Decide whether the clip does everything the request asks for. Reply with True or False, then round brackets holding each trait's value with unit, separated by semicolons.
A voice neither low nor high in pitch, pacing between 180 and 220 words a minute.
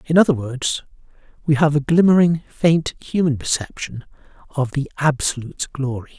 False (145 Hz; 135 wpm)